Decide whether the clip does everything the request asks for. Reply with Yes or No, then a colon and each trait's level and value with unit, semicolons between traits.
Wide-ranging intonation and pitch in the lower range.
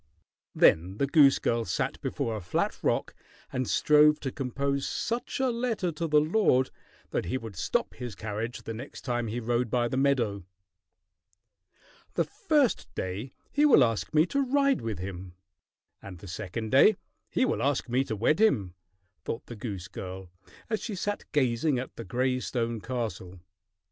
Yes: wide, 5.9 semitones; low, 125 Hz